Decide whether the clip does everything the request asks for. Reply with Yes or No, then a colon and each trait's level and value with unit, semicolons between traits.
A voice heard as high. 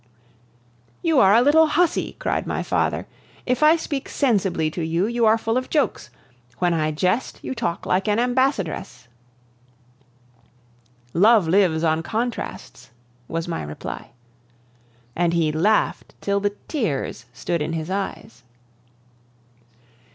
Yes: high, 195 Hz